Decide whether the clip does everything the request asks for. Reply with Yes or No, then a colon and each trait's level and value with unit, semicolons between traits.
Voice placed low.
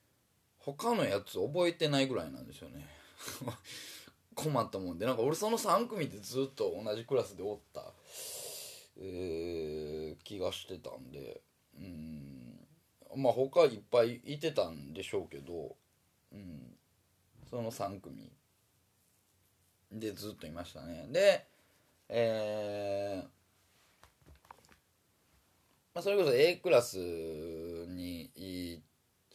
Yes: low, 100 Hz